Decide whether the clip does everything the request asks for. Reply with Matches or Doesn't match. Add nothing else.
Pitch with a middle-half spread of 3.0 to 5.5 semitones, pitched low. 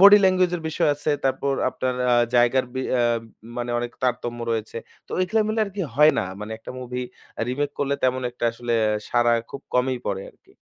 Matches